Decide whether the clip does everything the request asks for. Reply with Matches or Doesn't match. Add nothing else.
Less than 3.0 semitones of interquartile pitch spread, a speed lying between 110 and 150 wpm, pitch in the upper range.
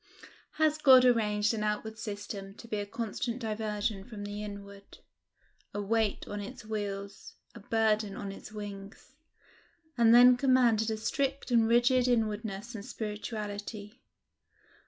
Matches